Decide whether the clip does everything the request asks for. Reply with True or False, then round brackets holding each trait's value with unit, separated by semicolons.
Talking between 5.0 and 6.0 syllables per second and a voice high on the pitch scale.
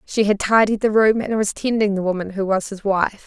True (5.4 syllables/s; 205 Hz)